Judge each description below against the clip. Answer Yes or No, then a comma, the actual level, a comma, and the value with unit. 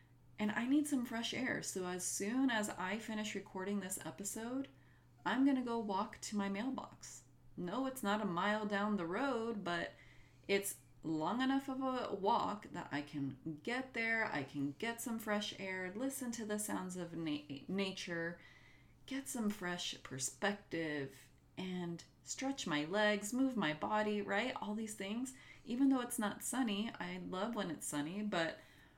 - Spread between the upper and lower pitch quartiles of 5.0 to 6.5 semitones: Yes, average, 5.3 semitones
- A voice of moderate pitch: No, high, 205 Hz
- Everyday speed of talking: Yes, average, 170 wpm